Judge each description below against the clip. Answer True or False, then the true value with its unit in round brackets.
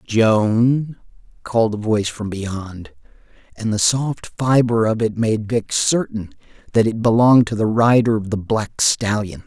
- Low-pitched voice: True (110 Hz)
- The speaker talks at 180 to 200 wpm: False (160 wpm)